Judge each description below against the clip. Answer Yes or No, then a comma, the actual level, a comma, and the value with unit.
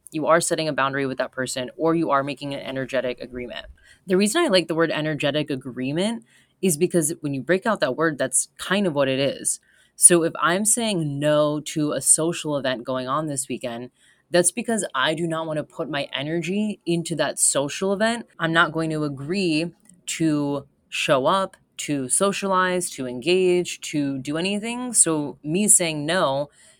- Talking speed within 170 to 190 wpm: Yes, average, 185 wpm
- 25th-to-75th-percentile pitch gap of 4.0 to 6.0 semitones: Yes, average, 4.3 semitones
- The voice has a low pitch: No, medium, 160 Hz